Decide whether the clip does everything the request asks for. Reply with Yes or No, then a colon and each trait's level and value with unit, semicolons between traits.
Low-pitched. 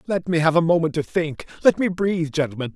No: medium, 165 Hz